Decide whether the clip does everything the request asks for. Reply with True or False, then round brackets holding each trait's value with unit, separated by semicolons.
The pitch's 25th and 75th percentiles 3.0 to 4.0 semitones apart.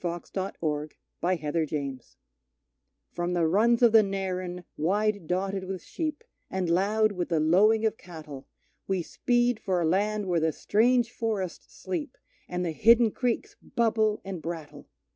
False (4.4 semitones)